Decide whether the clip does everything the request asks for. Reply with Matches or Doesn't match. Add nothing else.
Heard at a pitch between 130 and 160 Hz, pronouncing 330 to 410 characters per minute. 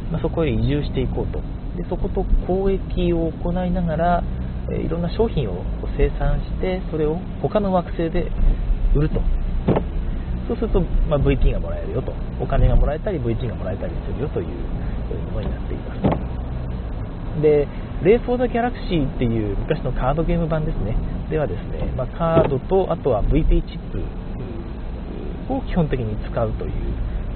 Matches